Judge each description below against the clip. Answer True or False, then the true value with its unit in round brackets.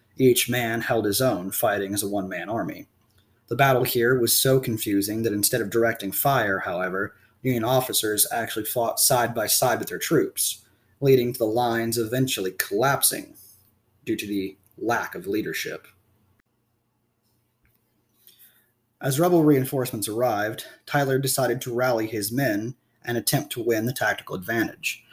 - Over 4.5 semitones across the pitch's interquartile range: False (2.8 semitones)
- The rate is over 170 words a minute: False (150 wpm)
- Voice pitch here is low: True (115 Hz)